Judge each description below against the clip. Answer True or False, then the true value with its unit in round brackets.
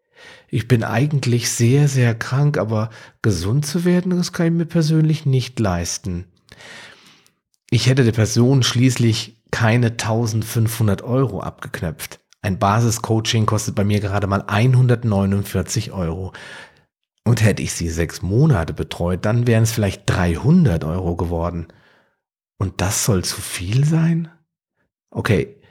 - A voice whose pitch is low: True (115 Hz)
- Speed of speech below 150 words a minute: True (130 wpm)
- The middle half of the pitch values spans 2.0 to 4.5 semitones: False (5.0 semitones)